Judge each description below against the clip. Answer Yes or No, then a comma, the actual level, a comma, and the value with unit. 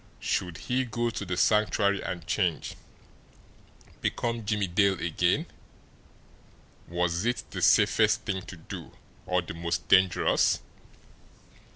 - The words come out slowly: Yes, slow, 115 wpm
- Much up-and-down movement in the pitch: No, average, 3.6 semitones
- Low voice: Yes, very low, 95 Hz